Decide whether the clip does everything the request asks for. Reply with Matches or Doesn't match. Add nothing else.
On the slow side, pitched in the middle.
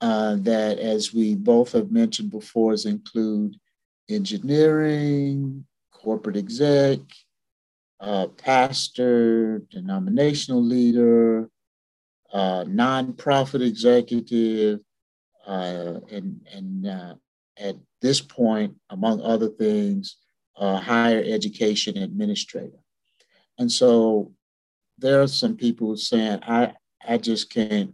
Doesn't match